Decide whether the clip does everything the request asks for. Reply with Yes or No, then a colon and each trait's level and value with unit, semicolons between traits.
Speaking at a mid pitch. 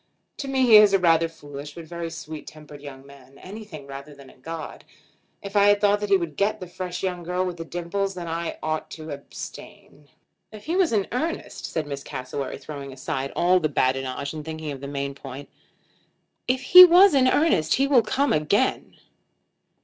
Yes: medium, 165 Hz